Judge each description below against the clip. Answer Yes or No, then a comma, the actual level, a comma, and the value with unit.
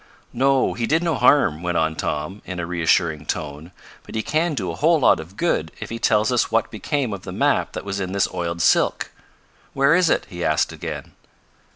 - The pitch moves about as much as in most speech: No, wide, 8.2 semitones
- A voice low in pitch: Yes, low, 100 Hz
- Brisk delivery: Yes, fast, 215 wpm